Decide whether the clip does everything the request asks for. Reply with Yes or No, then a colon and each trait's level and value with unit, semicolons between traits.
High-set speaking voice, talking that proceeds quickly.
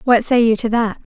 Yes: high, 230 Hz; fast, 260 wpm